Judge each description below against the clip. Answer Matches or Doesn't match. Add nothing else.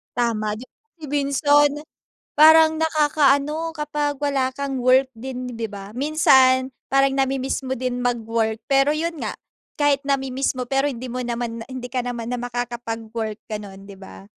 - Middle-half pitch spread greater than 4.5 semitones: Doesn't match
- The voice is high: Matches